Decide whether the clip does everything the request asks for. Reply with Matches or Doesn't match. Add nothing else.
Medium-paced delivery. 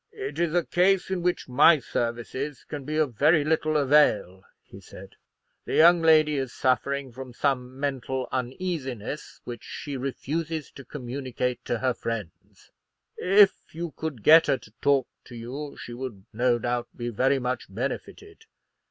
Matches